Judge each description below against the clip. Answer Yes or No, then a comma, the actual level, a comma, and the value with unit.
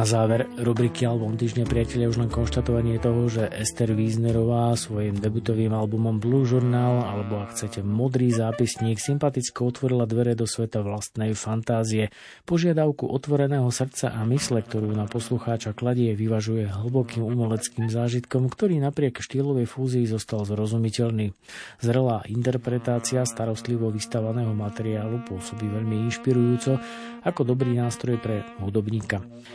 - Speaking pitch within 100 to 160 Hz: Yes, low, 115 Hz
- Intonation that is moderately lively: No, narrow, 1.9 semitones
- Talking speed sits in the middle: Yes, average, 125 wpm